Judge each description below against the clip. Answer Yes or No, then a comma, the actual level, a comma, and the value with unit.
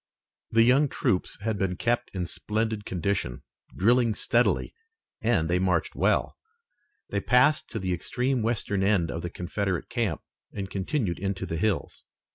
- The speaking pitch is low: Yes, low, 100 Hz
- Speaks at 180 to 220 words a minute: No, average, 150 wpm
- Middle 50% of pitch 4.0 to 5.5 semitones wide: Yes, average, 4.3 semitones